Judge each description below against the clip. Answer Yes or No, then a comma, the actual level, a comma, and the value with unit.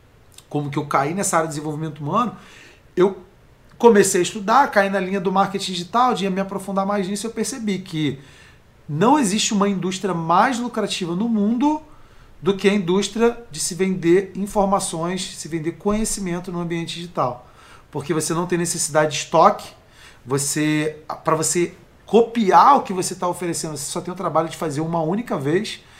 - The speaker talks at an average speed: Yes, average, 175 wpm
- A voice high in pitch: No, medium, 180 Hz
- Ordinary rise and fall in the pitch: Yes, average, 4.1 semitones